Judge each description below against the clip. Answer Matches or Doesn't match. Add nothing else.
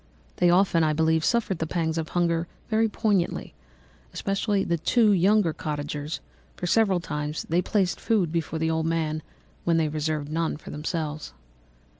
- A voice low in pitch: Doesn't match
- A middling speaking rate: Matches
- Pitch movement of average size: Matches